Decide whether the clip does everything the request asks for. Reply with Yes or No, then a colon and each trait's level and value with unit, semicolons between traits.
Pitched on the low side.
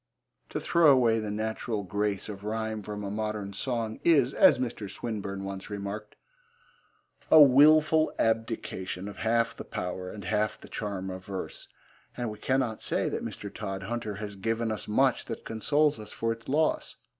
Yes: low, 110 Hz